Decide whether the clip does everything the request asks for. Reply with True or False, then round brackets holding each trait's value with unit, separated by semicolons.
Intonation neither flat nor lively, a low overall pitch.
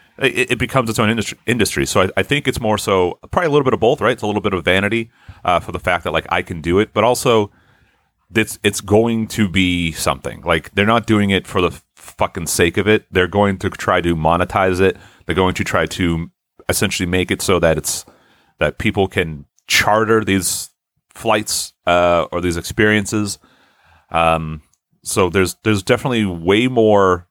True (3.6 semitones; 95 Hz)